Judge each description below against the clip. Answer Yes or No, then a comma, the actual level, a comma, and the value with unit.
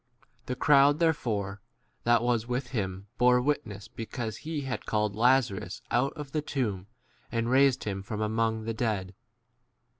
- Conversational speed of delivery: Yes, average, 160 wpm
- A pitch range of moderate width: Yes, average, 3.9 semitones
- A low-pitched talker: Yes, low, 115 Hz